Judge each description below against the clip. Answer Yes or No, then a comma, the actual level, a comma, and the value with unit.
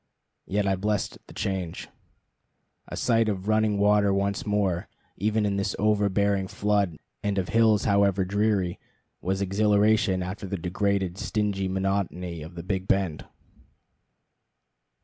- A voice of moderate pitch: No, low, 100 Hz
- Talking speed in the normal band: No, slow, 130 wpm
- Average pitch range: No, narrow, 1.7 semitones